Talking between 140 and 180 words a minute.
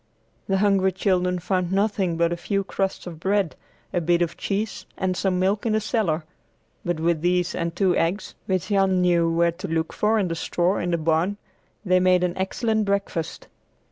No: average, 195 wpm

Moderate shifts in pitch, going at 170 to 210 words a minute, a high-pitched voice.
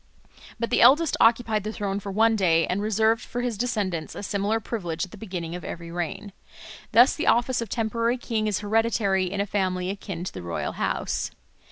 Yes: average, 3.5 semitones; average, 200 wpm; high, 205 Hz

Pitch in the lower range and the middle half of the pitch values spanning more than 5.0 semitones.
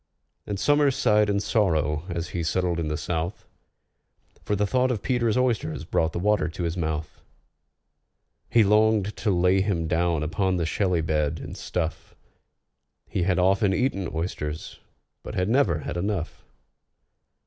No: very low, 90 Hz; average, 4.3 semitones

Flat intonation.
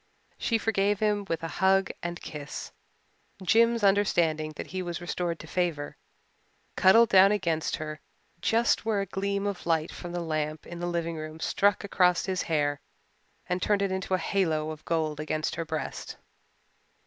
No: average, 3.9 semitones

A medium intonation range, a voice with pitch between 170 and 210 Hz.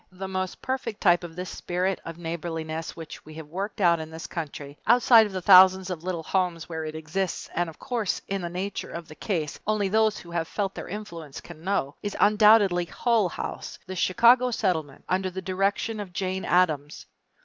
Yes: average, 3.5 semitones; medium, 185 Hz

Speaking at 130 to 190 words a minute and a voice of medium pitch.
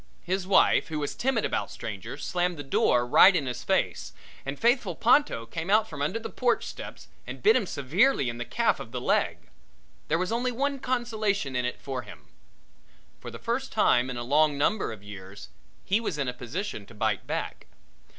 No: average, 200 wpm; medium, 160 Hz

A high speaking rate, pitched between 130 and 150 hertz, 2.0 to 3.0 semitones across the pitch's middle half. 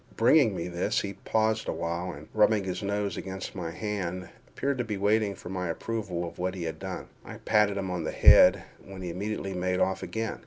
No: fast, 210 wpm; very low, 95 Hz; average, 2.7 semitones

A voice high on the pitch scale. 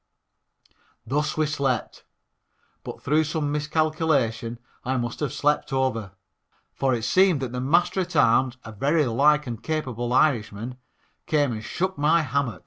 No: medium, 140 Hz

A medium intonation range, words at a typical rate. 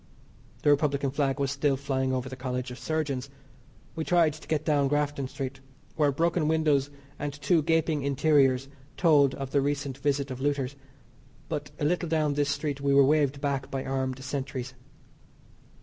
No: narrow, 1.8 semitones; average, 170 wpm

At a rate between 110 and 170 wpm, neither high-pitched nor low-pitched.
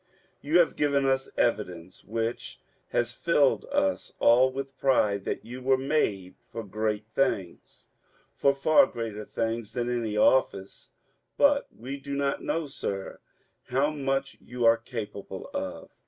No: average, 140 wpm; low, 125 Hz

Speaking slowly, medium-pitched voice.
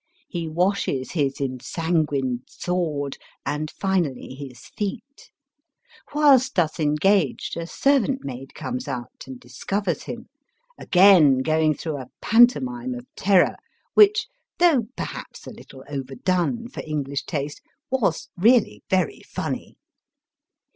Yes: slow, 115 wpm; medium, 175 Hz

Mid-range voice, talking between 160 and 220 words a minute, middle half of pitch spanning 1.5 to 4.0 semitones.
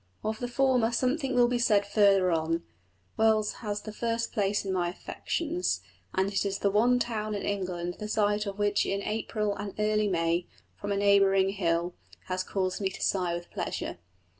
No: high, 205 Hz; average, 185 wpm; narrow, 2.5 semitones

